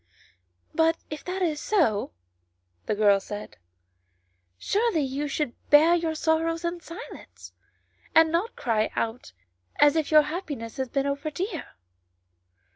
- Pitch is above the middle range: Yes, very high, 300 Hz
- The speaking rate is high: No, average, 140 wpm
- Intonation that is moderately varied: No, wide, 6.2 semitones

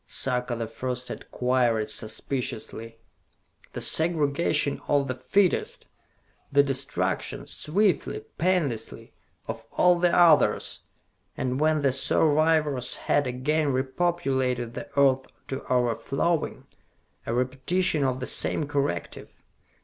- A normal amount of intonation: Yes, average, 3.7 semitones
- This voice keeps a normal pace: No, slow, 110 wpm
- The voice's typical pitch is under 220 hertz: Yes, low, 135 Hz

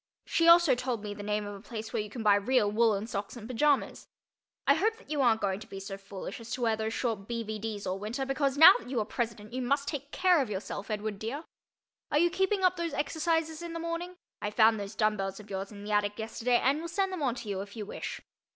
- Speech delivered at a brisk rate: Yes, fast, 265 wpm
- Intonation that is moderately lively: No, wide, 5.8 semitones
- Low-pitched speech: No, high, 225 Hz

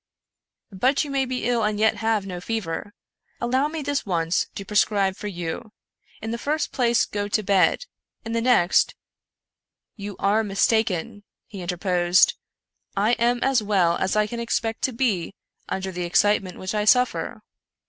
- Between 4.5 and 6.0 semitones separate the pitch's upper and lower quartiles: No, average, 3.9 semitones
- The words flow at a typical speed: Yes, average, 180 wpm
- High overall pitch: Yes, high, 210 Hz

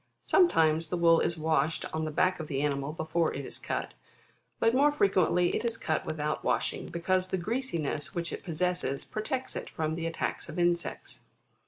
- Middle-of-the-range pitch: Yes, medium, 170 Hz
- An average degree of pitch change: Yes, average, 3.0 semitones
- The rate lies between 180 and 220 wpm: Yes, average, 190 wpm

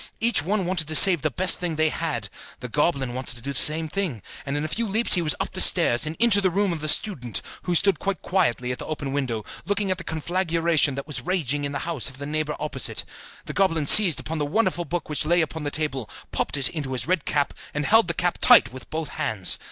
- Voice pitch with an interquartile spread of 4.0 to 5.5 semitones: Yes, average, 4.3 semitones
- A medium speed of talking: No, fast, 255 wpm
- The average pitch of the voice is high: No, medium, 155 Hz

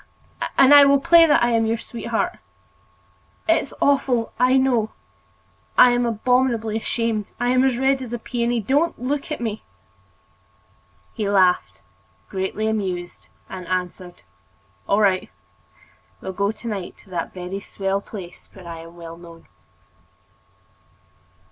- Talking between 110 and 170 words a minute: Yes, average, 140 wpm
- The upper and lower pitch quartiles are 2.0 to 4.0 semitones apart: No, average, 5.0 semitones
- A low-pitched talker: No, high, 220 Hz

